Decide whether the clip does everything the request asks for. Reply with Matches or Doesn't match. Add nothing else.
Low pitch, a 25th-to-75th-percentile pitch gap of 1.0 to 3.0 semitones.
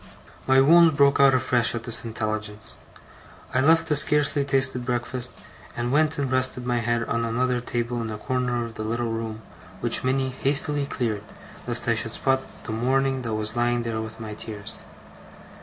Matches